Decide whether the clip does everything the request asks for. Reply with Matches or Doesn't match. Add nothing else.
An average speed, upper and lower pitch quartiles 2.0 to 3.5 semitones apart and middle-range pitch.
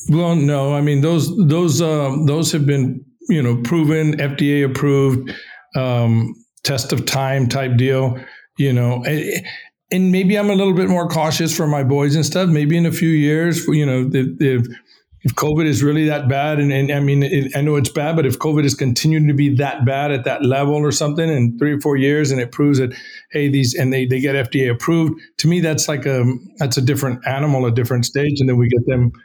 Doesn't match